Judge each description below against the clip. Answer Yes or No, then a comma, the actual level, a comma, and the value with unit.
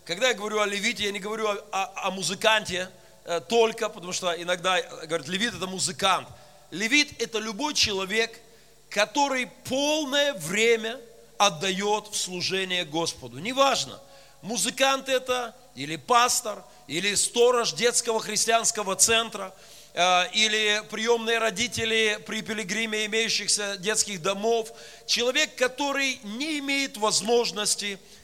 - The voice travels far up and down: No, average, 3.7 semitones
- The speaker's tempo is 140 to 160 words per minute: No, average, 115 wpm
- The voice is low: No, high, 215 Hz